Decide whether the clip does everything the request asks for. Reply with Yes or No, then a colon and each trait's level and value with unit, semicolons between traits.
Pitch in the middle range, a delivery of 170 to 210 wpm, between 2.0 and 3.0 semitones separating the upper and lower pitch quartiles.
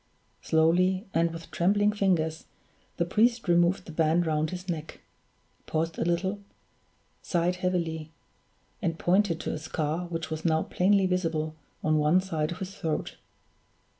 No: medium, 170 Hz; average, 145 wpm; narrow, 2.5 semitones